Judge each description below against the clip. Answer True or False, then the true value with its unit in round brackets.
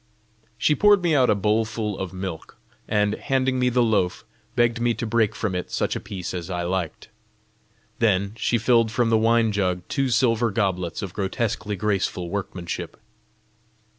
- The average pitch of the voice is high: False (105 Hz)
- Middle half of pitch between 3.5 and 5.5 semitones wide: True (3.8 semitones)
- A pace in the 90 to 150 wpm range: False (165 wpm)